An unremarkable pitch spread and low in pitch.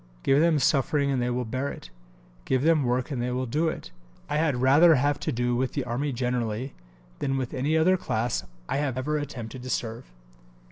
Yes: average, 3.1 semitones; low, 130 Hz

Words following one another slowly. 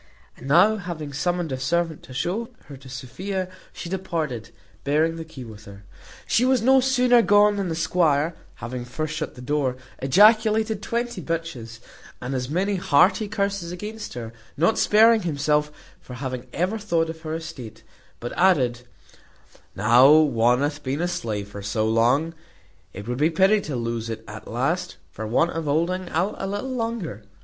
No: average, 170 wpm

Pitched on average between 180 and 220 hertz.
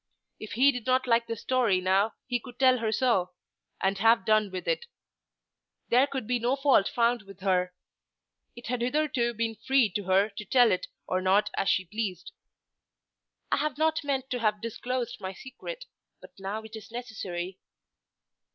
No: high, 230 Hz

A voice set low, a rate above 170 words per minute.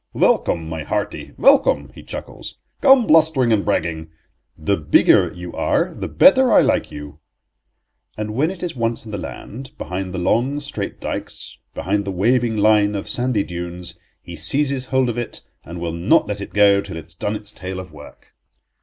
Yes: low, 105 Hz; average, 185 wpm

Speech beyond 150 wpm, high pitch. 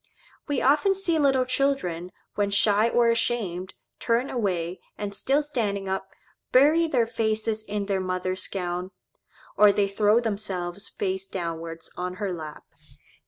No: average, 140 wpm; high, 205 Hz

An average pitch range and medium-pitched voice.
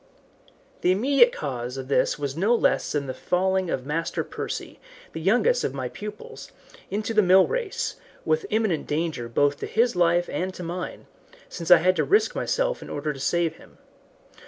No: wide, 6.3 semitones; medium, 180 Hz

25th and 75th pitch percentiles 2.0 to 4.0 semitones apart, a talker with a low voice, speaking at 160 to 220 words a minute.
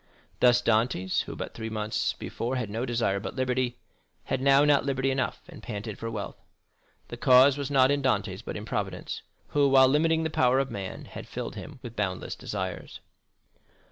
Yes: average, 3.4 semitones; low, 130 Hz; average, 185 wpm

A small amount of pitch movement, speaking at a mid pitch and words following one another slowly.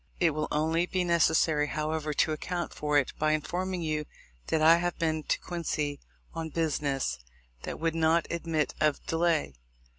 No: narrow, 1.8 semitones; medium, 160 Hz; average, 160 wpm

